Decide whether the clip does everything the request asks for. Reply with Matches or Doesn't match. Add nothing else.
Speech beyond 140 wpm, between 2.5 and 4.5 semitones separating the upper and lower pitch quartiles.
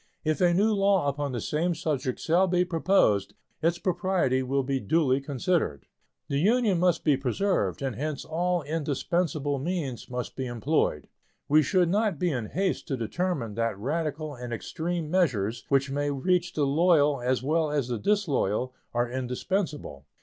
Doesn't match